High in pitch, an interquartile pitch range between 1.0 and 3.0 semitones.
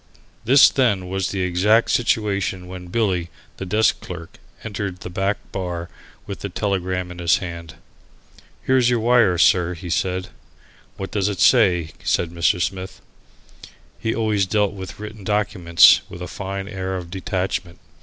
No: very low, 95 Hz; average, 2.7 semitones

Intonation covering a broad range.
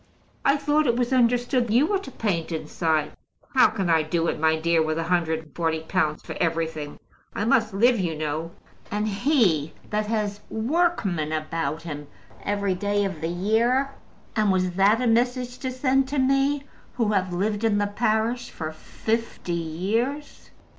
Yes: wide, 6.8 semitones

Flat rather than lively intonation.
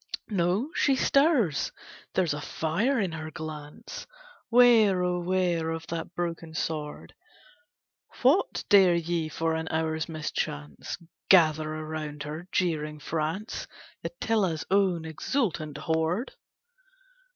No: average, 3.4 semitones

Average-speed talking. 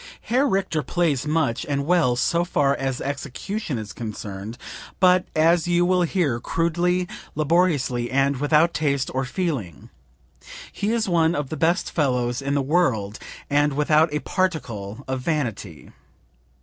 Yes: average, 145 wpm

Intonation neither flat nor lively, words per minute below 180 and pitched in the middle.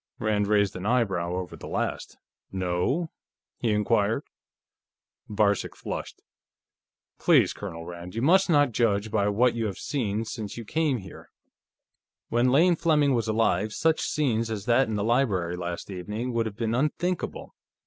No: average, 4.1 semitones; average, 155 wpm; low, 110 Hz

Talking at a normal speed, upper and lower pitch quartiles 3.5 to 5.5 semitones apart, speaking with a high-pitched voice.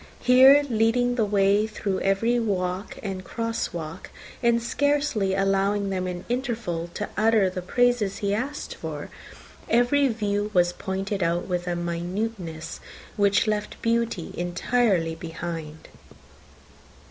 No: slow, 125 wpm; average, 4.4 semitones; high, 200 Hz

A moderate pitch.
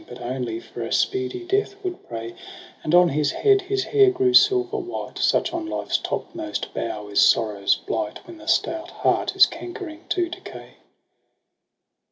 No: very high, 340 Hz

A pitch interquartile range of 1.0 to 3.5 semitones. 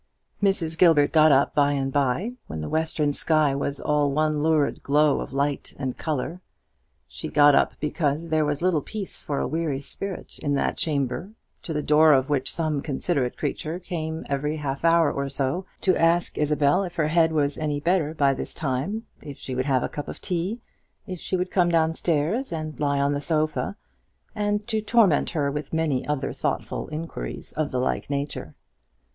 Yes: average, 2.8 semitones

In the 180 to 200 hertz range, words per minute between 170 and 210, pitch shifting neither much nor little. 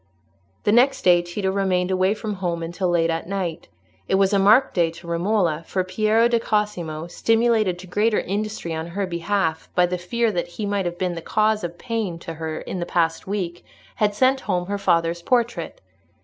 Yes: medium, 185 Hz; average, 200 wpm; average, 3.6 semitones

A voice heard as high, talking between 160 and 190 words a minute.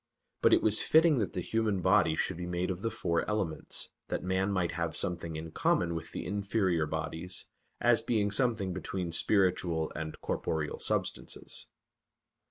No: very low, 90 Hz; average, 165 wpm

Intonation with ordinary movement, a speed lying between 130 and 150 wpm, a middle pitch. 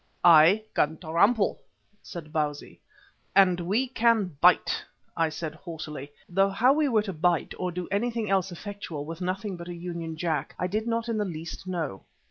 No: average, 4.0 semitones; average, 175 wpm; medium, 180 Hz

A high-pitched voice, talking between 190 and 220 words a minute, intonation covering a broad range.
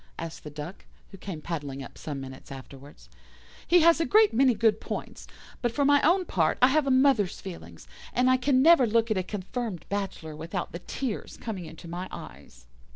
Yes: high, 200 Hz; average, 200 wpm; wide, 8.3 semitones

